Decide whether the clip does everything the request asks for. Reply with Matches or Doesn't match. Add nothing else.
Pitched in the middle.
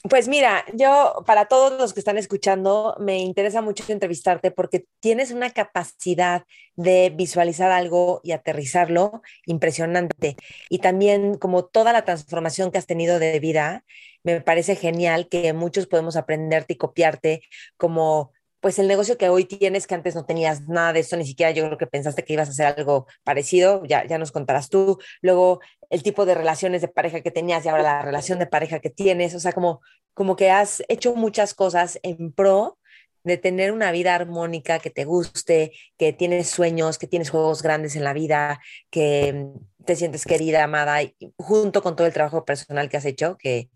Matches